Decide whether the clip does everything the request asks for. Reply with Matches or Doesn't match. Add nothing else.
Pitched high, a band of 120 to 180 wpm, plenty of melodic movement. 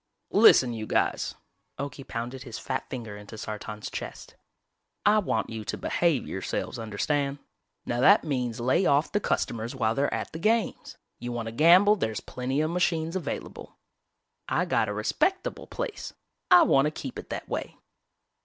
Doesn't match